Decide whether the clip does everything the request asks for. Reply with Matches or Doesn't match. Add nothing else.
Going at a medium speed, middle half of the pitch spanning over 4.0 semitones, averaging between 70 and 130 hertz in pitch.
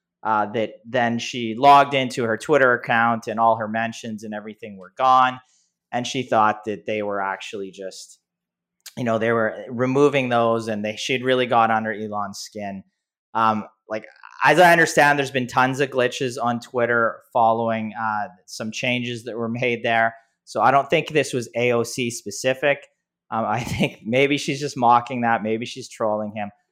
Doesn't match